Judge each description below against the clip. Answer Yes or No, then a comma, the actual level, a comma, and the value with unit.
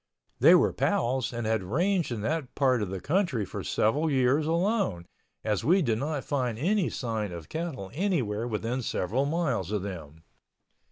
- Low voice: Yes, low, 125 Hz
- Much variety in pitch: Yes, wide, 7.1 semitones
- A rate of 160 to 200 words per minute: Yes, average, 170 wpm